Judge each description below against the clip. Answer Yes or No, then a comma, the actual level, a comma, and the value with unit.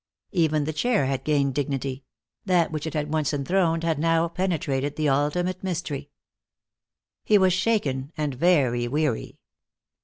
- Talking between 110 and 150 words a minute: Yes, average, 145 wpm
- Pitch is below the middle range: No, medium, 155 Hz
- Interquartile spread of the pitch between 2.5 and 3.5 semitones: No, average, 3.9 semitones